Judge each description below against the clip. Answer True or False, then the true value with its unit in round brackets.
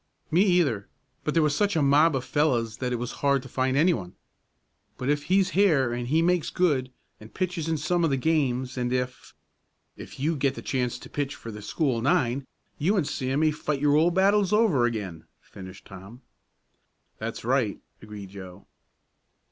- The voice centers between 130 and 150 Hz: True (140 Hz)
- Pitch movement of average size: True (5.0 semitones)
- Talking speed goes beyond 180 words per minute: True (190 wpm)